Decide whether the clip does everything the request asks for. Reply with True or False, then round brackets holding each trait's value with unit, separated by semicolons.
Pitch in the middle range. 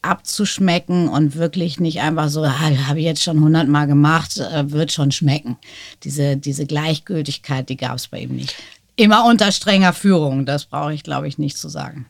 True (150 Hz)